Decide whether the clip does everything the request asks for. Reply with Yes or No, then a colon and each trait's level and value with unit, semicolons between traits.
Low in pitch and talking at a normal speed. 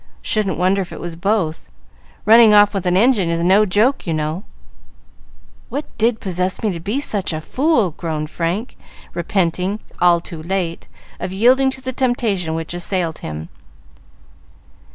No: high, 190 Hz; average, 155 wpm